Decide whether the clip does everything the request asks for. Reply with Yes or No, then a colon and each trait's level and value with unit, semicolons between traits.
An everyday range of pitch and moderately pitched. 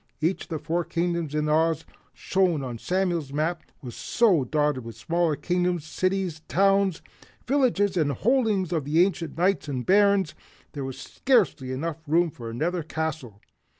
Yes: average, 4.1 semitones; medium, 165 Hz